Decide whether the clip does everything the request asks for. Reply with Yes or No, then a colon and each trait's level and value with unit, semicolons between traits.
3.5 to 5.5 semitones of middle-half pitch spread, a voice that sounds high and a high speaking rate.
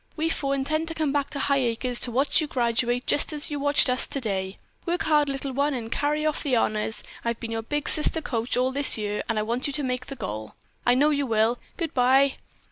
Yes: average, 3.8 semitones; very high, 270 Hz; fast, 230 wpm